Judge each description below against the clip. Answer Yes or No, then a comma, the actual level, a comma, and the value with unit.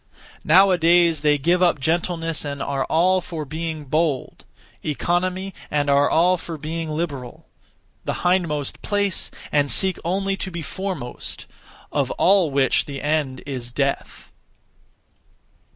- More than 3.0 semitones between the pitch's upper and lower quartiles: Yes, average, 3.8 semitones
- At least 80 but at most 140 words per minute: Yes, slow, 135 wpm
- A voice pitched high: No, medium, 160 Hz